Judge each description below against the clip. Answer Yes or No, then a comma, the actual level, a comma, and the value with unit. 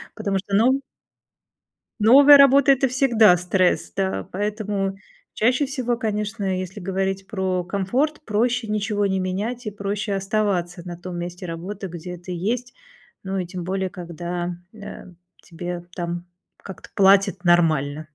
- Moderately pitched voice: No, high, 195 Hz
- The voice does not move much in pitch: No, average, 3.4 semitones